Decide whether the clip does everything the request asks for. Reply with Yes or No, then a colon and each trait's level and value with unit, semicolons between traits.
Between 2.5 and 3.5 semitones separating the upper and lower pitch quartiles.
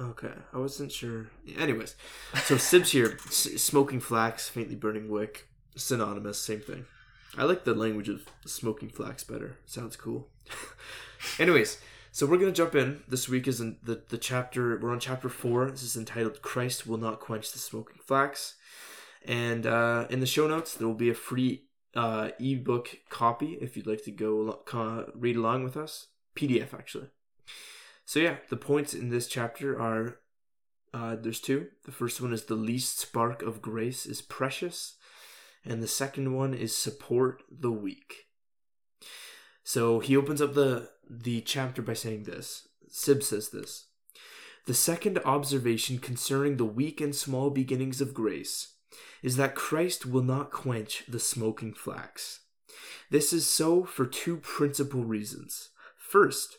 Yes: average, 3.2 semitones